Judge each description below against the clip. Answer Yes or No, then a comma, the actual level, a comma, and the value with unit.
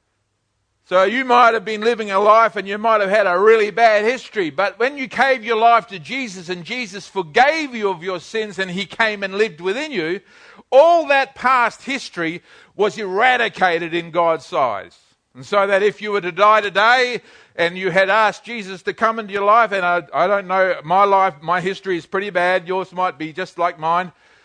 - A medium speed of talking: No, fast, 210 wpm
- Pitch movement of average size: Yes, average, 3.6 semitones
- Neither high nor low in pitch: No, high, 200 Hz